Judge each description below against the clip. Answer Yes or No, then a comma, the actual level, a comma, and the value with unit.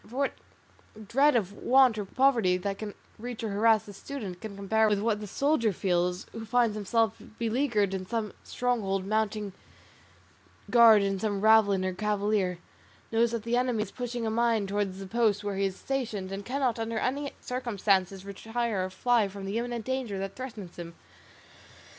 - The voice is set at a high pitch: Yes, high, 215 Hz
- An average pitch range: Yes, average, 3.1 semitones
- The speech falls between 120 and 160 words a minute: No, average, 175 wpm